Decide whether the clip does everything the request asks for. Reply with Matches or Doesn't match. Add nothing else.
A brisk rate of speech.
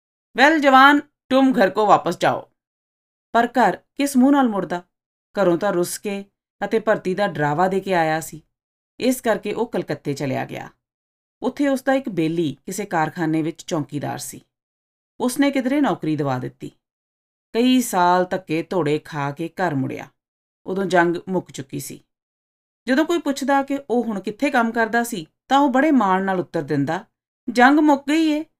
Matches